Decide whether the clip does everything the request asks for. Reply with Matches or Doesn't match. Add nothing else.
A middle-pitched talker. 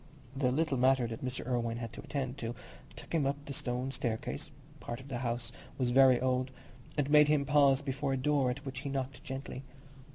Doesn't match